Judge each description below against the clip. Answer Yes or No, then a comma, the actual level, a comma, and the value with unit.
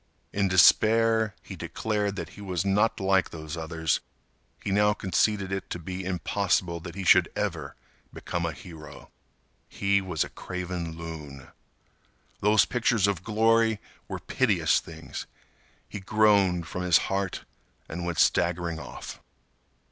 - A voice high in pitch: No, very low, 95 Hz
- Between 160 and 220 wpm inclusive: No, average, 140 wpm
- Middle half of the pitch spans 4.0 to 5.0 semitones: No, average, 3.4 semitones